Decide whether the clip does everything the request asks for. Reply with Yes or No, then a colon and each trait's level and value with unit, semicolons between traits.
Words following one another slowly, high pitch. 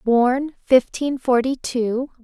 Yes: slow, 105 wpm; very high, 255 Hz